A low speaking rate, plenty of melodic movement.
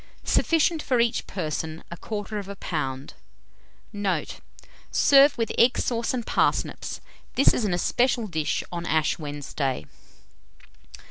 Yes: slow, 115 wpm; wide, 7.1 semitones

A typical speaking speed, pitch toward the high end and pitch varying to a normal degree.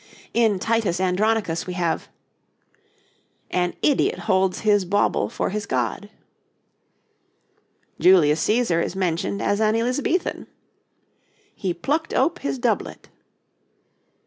No: slow, 105 wpm; high, 195 Hz; average, 4.0 semitones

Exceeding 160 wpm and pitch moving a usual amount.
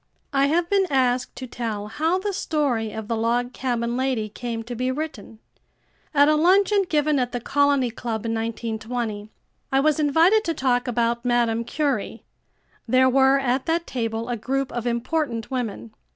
Yes: average, 170 wpm; average, 3.8 semitones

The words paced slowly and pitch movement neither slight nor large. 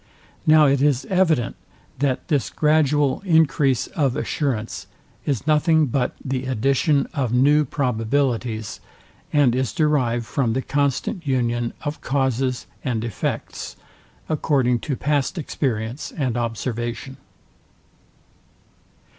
Yes: slow, 110 wpm; average, 3.4 semitones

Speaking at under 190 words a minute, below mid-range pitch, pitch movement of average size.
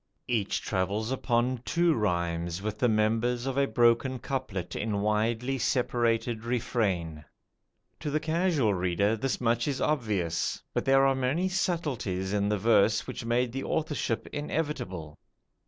Yes: average, 140 wpm; low, 115 Hz; average, 4.7 semitones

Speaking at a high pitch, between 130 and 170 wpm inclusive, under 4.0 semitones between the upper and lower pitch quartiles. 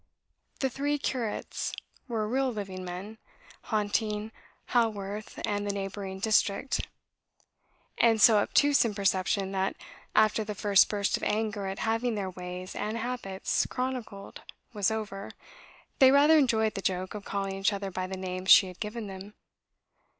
Yes: high, 210 Hz; average, 150 wpm; narrow, 2.5 semitones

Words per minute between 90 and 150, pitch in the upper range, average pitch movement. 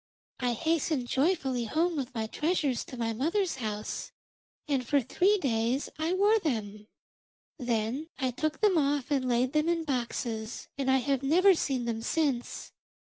No: average, 160 wpm; very high, 270 Hz; average, 5.0 semitones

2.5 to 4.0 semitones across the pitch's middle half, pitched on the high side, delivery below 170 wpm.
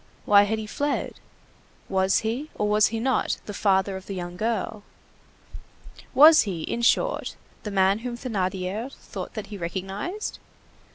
Yes: average, 3.5 semitones; high, 210 Hz; average, 155 wpm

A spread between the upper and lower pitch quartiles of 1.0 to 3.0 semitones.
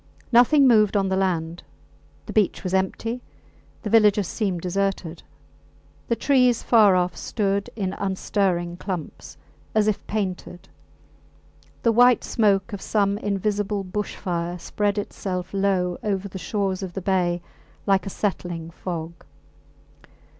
Yes: narrow, 2.5 semitones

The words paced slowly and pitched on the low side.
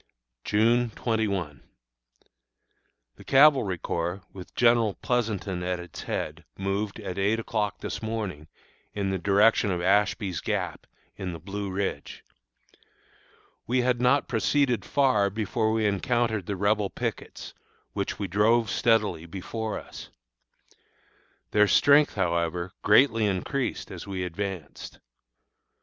Yes: slow, 120 wpm; low, 105 Hz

